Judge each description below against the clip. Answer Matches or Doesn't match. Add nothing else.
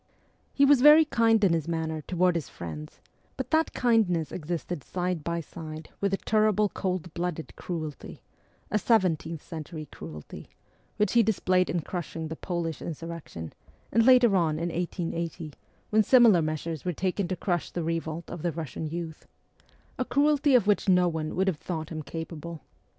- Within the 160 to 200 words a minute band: Matches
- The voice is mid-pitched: Matches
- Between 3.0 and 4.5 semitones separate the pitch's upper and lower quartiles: Matches